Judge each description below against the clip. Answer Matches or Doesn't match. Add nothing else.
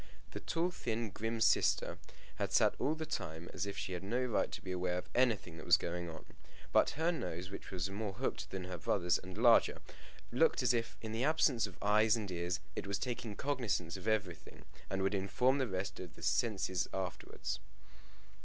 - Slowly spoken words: Doesn't match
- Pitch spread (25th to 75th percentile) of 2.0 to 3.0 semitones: Doesn't match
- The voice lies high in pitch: Doesn't match